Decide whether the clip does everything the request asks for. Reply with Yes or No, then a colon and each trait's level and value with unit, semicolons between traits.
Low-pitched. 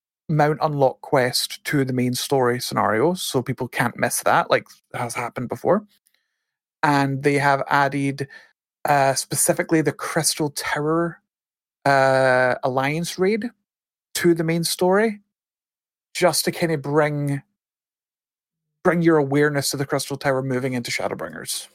No: medium, 145 Hz